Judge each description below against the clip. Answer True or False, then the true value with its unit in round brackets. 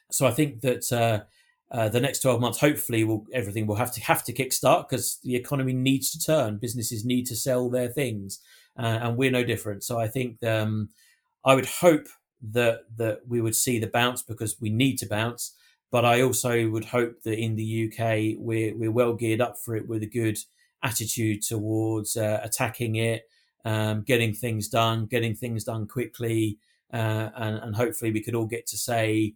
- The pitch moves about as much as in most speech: False (2.1 semitones)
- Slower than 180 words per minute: False (200 wpm)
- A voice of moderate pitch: False (115 Hz)